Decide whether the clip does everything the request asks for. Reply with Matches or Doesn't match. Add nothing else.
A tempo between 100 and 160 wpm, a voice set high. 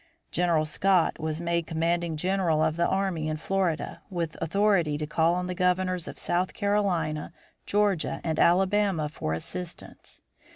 Doesn't match